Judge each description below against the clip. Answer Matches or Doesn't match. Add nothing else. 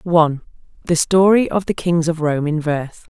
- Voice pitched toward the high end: Doesn't match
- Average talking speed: Matches